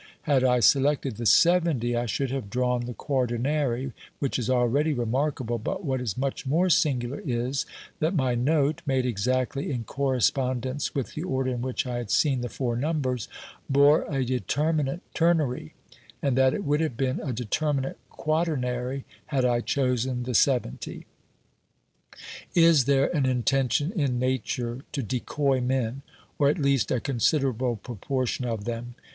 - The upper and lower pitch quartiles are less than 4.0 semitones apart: Yes, average, 2.7 semitones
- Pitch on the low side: Yes, low, 130 Hz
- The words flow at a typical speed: Yes, average, 155 wpm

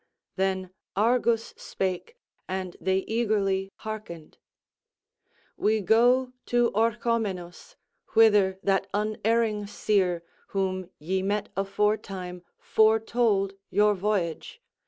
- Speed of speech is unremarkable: No, slow, 90 wpm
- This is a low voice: No, high, 205 Hz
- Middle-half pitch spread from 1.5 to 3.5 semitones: Yes, average, 2.7 semitones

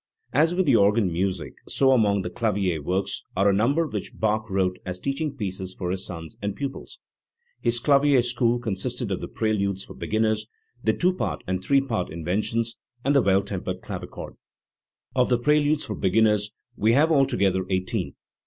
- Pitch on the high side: No, low, 110 Hz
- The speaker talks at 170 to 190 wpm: Yes, average, 175 wpm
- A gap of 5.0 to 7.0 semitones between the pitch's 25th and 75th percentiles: Yes, wide, 5.5 semitones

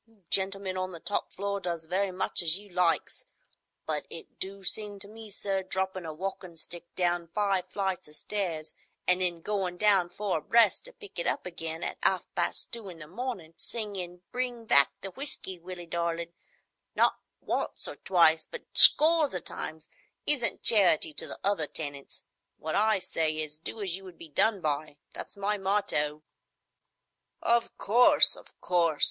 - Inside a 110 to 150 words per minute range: No, average, 170 wpm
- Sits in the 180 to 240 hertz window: Yes, medium, 185 Hz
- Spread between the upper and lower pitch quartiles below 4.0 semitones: Yes, average, 3.6 semitones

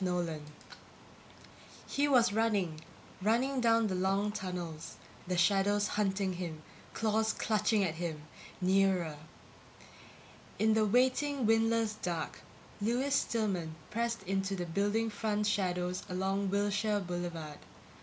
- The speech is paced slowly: Yes, slow, 115 wpm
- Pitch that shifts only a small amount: No, average, 3.6 semitones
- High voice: Yes, high, 200 Hz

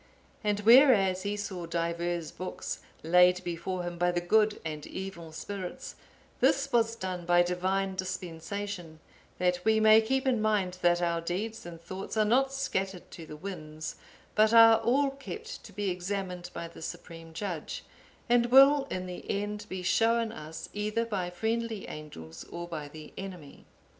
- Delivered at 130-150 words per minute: No, average, 165 wpm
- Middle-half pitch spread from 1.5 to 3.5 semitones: No, average, 4.0 semitones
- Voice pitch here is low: No, high, 190 Hz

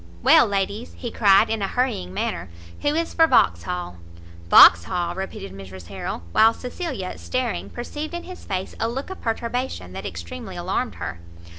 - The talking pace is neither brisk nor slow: Yes, average, 160 wpm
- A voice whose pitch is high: Yes, high, 200 Hz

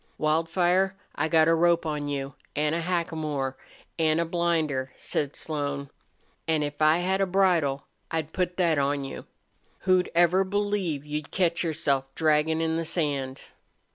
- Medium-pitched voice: Yes, medium, 160 Hz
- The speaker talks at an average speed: Yes, average, 155 wpm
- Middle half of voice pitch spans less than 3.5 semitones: Yes, average, 3.0 semitones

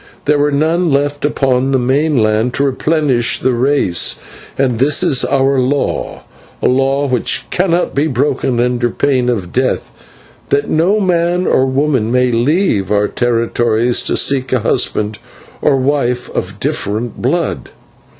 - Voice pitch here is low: Yes, low, 130 Hz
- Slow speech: No, average, 150 wpm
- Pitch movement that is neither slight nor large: Yes, average, 3.2 semitones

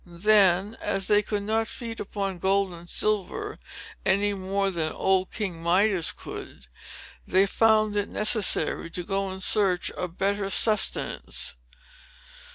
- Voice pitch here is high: Yes, high, 195 Hz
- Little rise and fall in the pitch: Yes, narrow, 2.2 semitones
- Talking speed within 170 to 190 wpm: No, slow, 135 wpm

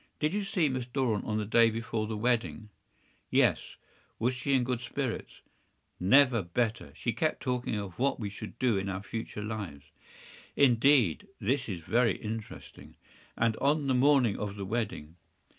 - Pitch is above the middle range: No, low, 115 Hz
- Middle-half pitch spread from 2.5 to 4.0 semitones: Yes, average, 3.6 semitones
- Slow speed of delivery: No, average, 165 wpm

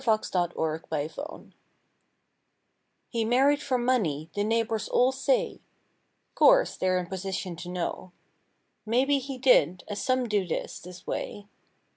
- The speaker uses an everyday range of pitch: No, wide, 6.1 semitones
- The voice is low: No, high, 215 Hz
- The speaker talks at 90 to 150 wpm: Yes, average, 140 wpm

